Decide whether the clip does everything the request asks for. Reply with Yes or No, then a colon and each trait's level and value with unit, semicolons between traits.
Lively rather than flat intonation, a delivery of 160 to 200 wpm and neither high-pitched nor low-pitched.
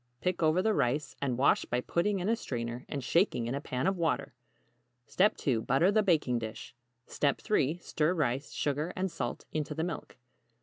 Yes: wide, 5.9 semitones; average, 180 wpm; medium, 150 Hz